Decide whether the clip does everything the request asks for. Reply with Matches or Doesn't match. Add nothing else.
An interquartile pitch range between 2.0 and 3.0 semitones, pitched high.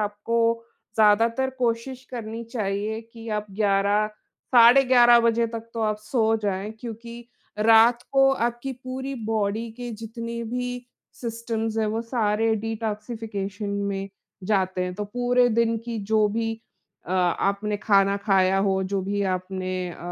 Matches